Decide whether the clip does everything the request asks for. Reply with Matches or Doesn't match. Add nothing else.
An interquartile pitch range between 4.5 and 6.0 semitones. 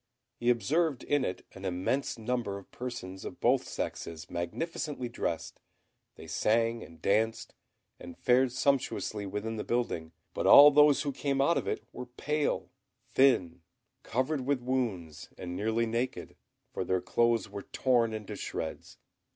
Matches